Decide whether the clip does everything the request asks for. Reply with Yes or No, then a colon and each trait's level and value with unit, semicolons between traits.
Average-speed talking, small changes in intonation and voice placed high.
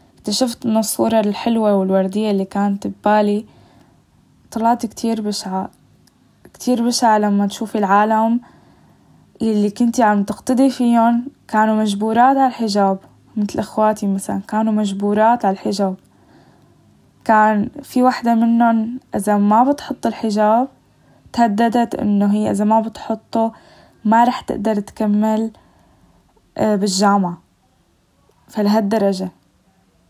Yes: average, 105 wpm; narrow, 2.1 semitones; high, 215 Hz